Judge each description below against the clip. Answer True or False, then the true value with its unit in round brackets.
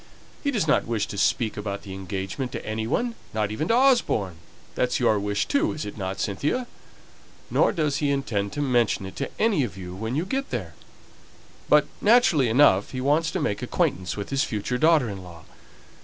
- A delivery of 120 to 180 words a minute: False (195 wpm)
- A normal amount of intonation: False (7.1 semitones)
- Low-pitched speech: True (120 Hz)